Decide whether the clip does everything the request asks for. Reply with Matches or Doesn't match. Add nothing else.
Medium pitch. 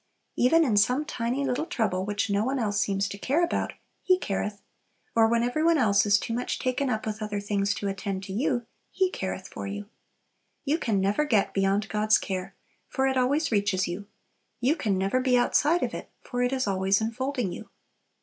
Doesn't match